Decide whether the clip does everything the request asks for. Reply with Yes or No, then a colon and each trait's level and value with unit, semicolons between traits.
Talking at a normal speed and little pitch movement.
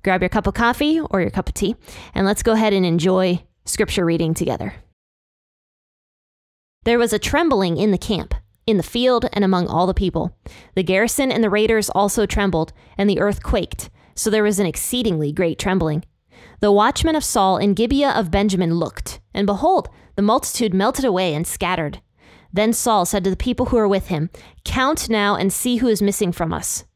No: average, 195 wpm; average, 3.8 semitones